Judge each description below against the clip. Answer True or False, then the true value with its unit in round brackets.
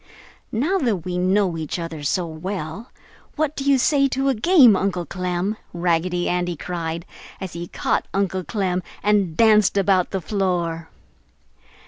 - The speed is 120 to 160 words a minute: True (150 wpm)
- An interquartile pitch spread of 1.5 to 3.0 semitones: False (3.7 semitones)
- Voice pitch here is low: False (185 Hz)